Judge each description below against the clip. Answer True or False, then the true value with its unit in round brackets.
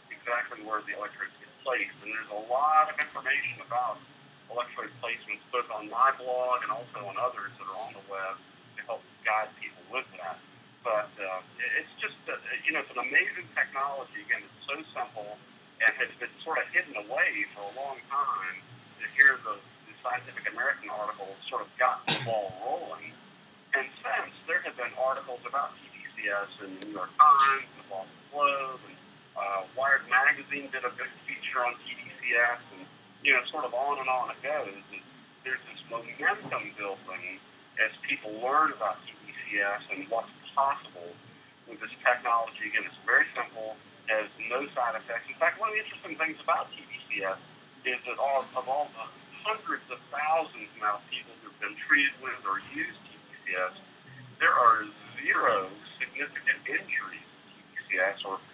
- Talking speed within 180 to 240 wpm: False (170 wpm)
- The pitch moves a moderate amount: True (4.8 semitones)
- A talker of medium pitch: False (125 Hz)